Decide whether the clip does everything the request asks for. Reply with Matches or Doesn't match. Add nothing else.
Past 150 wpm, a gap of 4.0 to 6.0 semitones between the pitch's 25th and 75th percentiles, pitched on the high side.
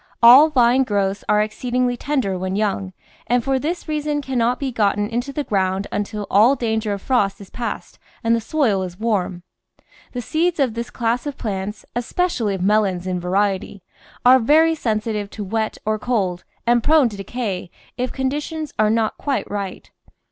Matches